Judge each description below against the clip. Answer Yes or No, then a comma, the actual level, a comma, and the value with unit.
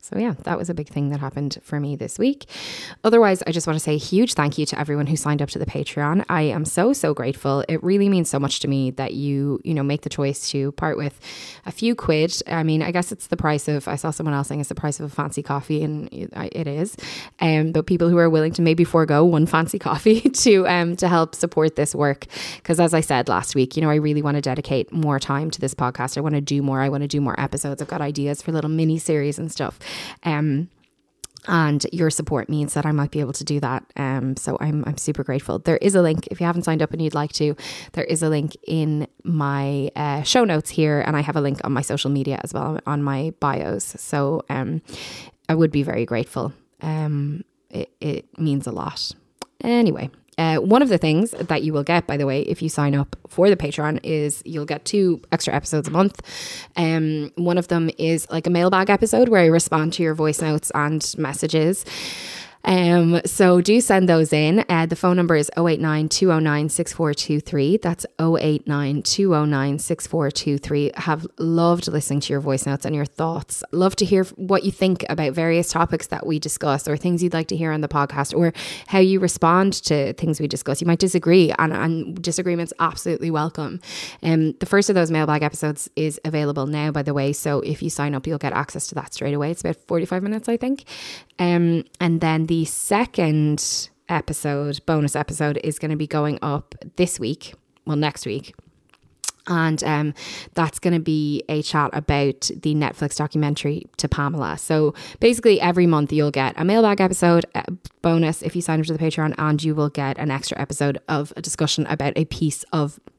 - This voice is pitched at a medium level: Yes, medium, 155 Hz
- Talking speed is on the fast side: Yes, fast, 220 wpm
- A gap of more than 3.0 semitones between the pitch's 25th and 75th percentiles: No, narrow, 2.6 semitones